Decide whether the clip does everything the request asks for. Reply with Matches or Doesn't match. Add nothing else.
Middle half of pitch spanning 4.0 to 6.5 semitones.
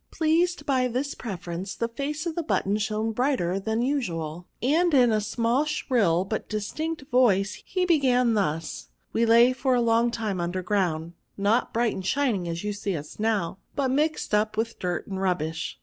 Matches